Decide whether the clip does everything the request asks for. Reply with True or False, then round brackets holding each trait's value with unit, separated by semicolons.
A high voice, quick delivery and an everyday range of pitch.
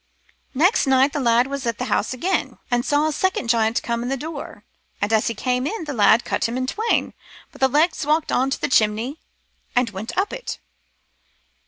True (260 Hz; 215 wpm; 4.4 semitones)